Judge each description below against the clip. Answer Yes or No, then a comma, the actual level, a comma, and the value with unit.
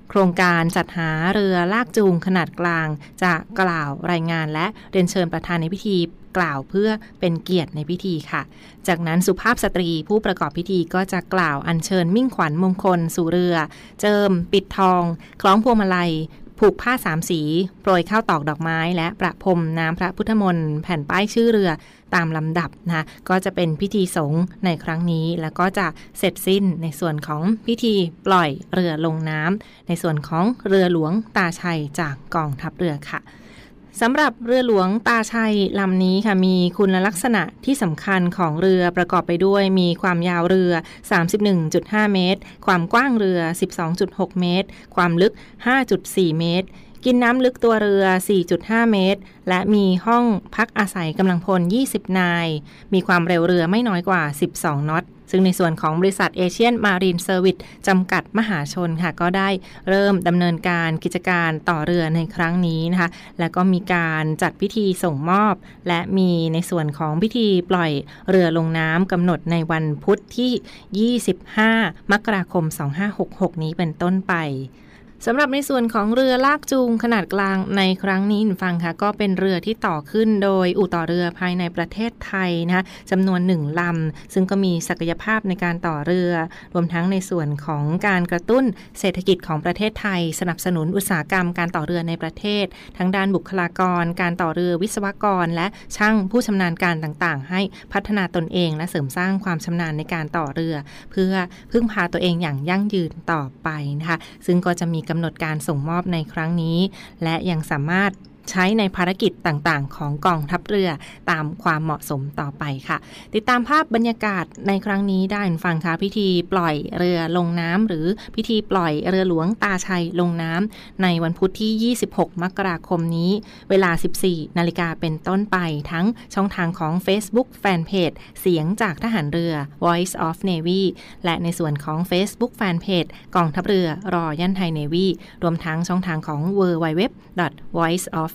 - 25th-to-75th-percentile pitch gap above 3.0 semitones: No, average, 2.7 semitones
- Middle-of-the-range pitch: Yes, medium, 180 Hz